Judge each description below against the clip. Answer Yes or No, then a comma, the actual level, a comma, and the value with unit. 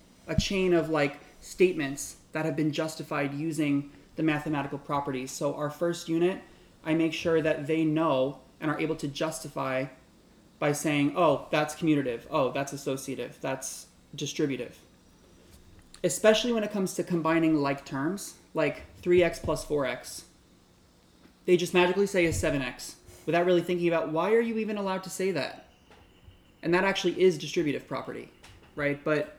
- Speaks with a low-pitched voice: No, medium, 155 Hz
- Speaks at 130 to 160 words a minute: Yes, average, 155 wpm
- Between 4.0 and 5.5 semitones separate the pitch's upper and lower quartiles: No, average, 3.6 semitones